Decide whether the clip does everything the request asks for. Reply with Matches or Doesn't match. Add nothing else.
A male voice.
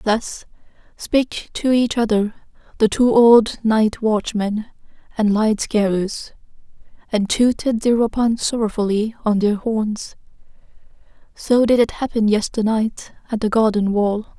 Doesn't match